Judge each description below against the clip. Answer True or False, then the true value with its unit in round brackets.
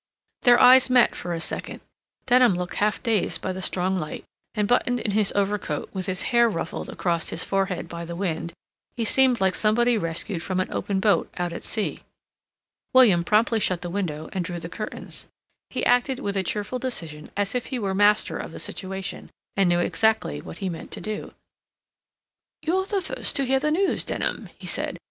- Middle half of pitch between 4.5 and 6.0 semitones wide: True (5.1 semitones)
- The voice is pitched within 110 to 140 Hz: False (200 Hz)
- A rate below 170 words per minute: False (195 wpm)